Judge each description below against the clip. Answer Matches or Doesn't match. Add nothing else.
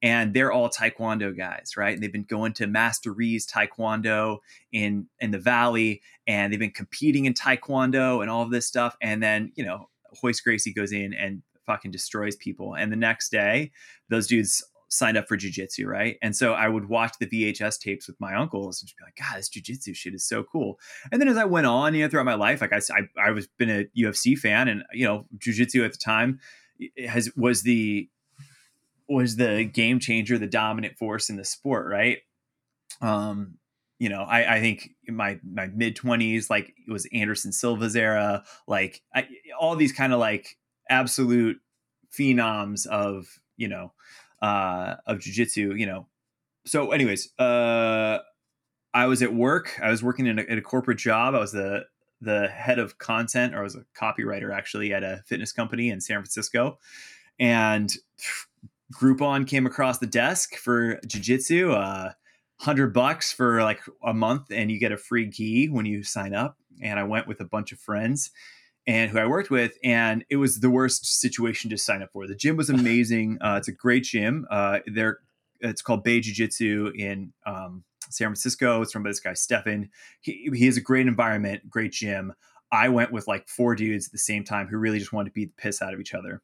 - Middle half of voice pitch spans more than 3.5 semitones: Doesn't match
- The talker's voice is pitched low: Matches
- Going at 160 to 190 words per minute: Doesn't match